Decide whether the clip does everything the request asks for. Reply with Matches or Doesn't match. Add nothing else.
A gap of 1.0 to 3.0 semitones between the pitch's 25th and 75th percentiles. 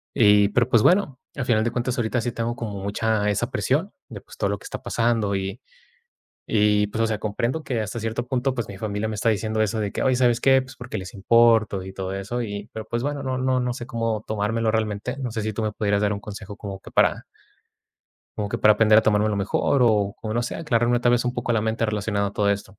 Matches